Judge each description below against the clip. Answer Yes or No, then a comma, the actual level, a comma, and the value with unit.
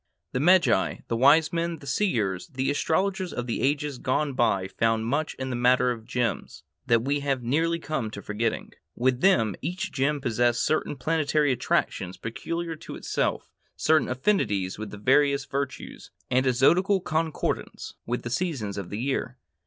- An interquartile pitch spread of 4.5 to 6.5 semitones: Yes, average, 4.9 semitones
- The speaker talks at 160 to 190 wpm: Yes, average, 170 wpm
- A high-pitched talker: No, low, 130 Hz